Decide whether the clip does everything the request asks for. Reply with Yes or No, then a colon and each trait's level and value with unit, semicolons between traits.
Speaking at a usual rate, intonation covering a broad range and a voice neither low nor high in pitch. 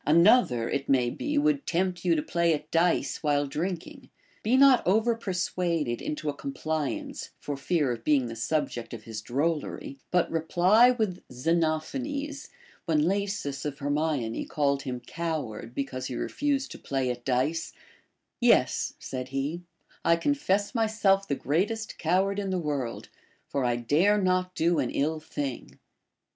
Yes: average, 155 wpm; wide, 5.9 semitones; medium, 160 Hz